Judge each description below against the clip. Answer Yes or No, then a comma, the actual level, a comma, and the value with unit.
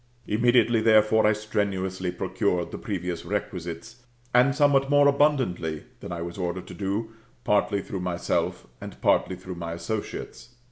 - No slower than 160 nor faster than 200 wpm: No, average, 145 wpm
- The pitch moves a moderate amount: Yes, average, 4.2 semitones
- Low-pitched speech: Yes, low, 100 Hz